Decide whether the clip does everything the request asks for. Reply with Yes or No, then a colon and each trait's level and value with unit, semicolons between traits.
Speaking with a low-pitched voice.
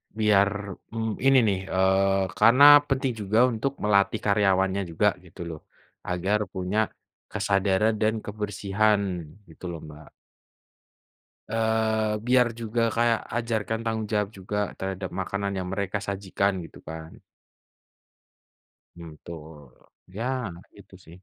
Yes: low, 100 Hz